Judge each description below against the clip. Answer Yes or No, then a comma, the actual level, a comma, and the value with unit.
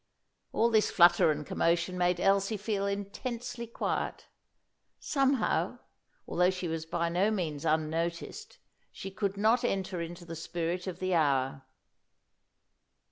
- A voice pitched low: No, medium, 180 Hz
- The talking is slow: Yes, slow, 130 wpm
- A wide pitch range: No, average, 3.5 semitones